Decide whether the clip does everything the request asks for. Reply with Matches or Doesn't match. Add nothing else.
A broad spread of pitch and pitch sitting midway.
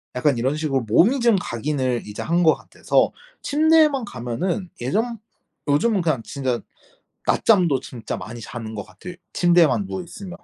Matches